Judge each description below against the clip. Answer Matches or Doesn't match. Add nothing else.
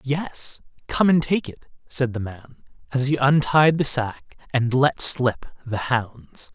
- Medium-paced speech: Matches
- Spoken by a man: Matches